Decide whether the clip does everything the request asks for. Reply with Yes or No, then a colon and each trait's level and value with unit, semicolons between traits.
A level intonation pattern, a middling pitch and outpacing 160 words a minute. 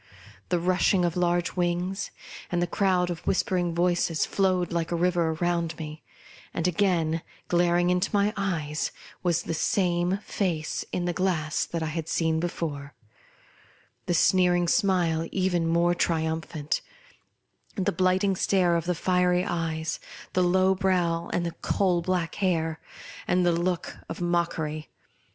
No: narrow, 1.7 semitones; medium, 175 Hz; average, 150 wpm